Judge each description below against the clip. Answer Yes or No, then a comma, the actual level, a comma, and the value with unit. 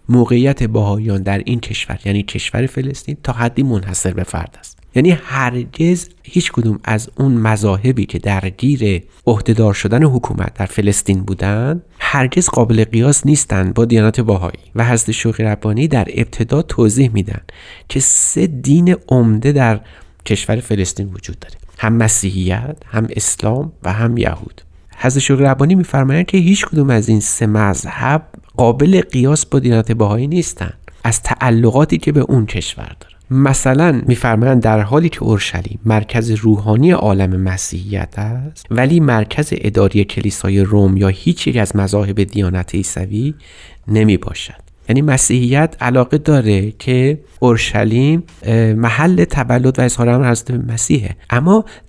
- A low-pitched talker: Yes, low, 115 Hz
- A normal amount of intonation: Yes, average, 4.7 semitones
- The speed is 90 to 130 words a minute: No, average, 140 wpm